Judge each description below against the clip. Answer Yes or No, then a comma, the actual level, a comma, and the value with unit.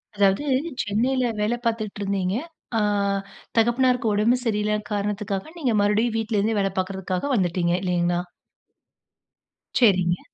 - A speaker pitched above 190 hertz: Yes, high, 210 Hz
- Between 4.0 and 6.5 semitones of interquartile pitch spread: No, average, 3.2 semitones